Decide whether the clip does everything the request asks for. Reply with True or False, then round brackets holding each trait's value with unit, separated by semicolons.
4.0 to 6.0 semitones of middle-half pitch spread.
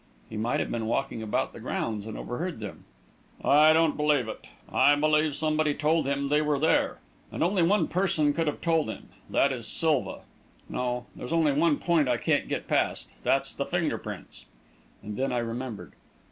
True (4.4 semitones)